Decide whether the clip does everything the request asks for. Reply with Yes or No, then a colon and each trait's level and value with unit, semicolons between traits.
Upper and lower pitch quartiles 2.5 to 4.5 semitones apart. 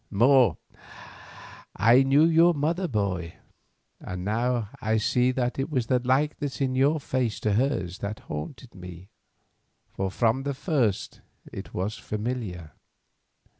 No: average, 5.1 semitones